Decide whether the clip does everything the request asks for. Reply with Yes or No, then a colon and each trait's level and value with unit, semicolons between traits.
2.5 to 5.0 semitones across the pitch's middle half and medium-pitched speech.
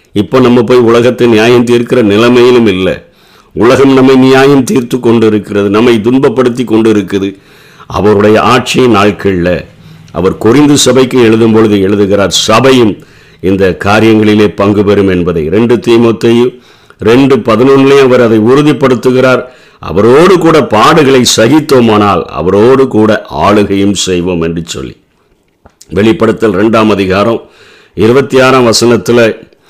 No: average, 3.7 semitones; low, 115 Hz